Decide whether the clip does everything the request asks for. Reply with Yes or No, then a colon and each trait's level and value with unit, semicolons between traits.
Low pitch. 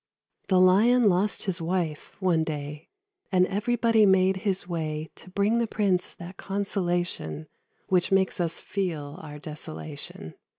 No: medium, 185 Hz